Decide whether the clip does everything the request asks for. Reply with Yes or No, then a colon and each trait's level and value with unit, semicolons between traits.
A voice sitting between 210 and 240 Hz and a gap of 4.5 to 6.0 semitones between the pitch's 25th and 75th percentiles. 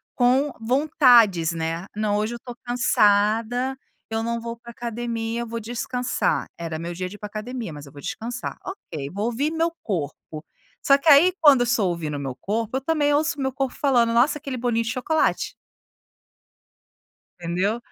No: high, 235 Hz; average, 4.1 semitones